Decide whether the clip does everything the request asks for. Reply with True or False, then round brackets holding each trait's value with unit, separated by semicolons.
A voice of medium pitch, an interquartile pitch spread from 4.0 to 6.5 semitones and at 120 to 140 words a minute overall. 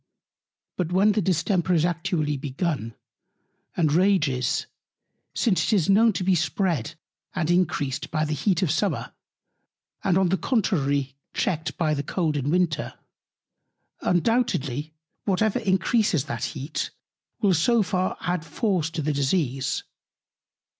True (170 Hz; 4.3 semitones; 135 wpm)